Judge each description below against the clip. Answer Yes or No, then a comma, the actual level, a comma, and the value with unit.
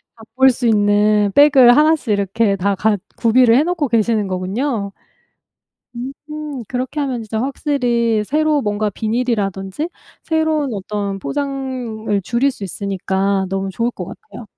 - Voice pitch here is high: Yes, high, 230 Hz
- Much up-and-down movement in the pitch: No, average, 4.9 semitones